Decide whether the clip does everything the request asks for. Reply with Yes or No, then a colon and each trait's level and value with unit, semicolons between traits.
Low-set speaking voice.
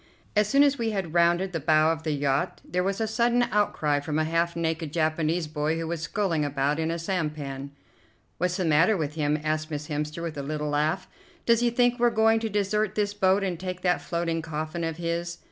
No: medium, 165 Hz